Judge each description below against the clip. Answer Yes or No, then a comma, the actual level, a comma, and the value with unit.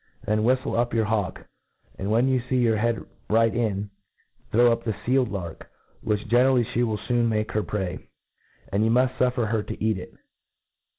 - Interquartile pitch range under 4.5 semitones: Yes, narrow, 2.4 semitones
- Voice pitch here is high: No, low, 115 Hz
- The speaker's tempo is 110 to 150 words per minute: No, average, 190 wpm